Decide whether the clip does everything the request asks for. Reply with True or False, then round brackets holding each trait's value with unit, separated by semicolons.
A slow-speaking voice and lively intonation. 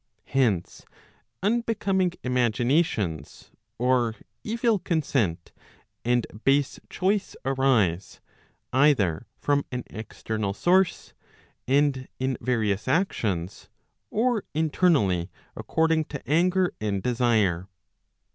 True (85 wpm; 7.5 semitones)